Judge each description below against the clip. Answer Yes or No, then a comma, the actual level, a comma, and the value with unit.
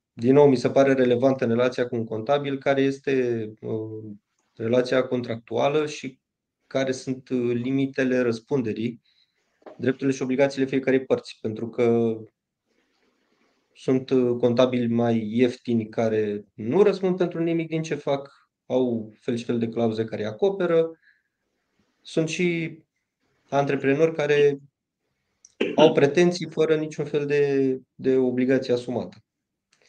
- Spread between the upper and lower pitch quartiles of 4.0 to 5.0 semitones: No, average, 3.2 semitones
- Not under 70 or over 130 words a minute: Yes, average, 120 wpm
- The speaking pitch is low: Yes, low, 130 Hz